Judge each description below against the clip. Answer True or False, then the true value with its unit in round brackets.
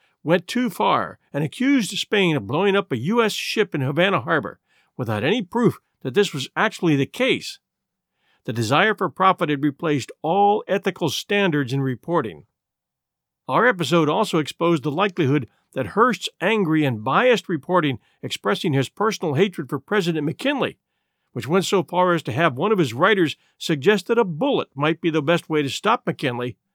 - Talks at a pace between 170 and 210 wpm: True (175 wpm)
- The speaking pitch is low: False (170 Hz)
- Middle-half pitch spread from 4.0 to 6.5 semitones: True (5.3 semitones)